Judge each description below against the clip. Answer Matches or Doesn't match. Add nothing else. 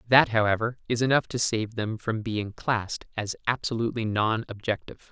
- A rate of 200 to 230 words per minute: Doesn't match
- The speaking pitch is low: Matches